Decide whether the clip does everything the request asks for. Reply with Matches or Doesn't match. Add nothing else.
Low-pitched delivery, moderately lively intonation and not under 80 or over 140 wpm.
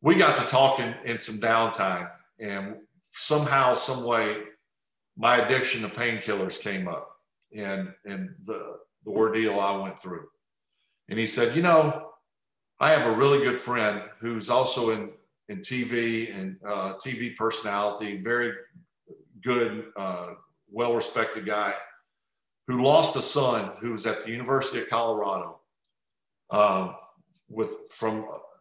Matches